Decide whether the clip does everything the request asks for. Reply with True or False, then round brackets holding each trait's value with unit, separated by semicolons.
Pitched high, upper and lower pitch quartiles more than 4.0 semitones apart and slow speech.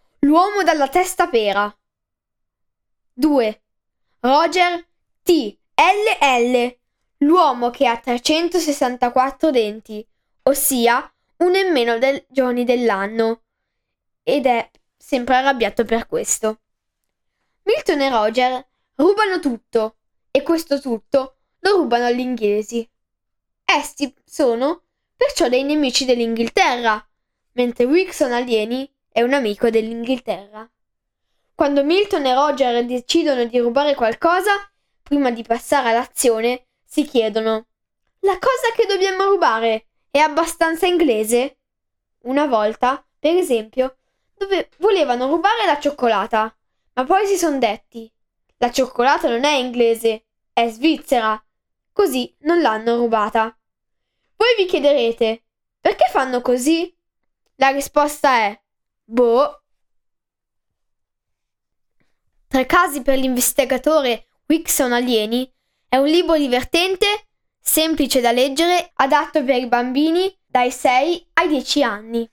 True (265 Hz; 5.3 semitones; 110 wpm)